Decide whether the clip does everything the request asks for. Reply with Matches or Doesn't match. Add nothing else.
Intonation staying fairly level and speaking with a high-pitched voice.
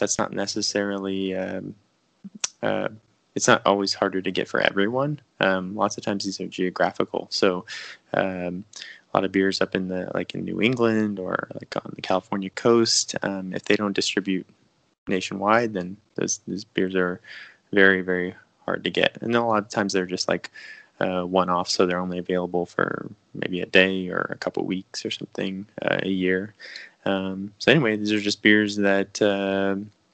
Doesn't match